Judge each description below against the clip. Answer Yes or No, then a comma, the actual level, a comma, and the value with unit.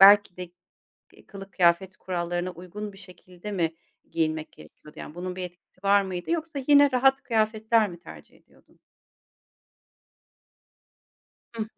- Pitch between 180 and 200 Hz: Yes, high, 190 Hz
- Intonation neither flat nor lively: Yes, average, 3.5 semitones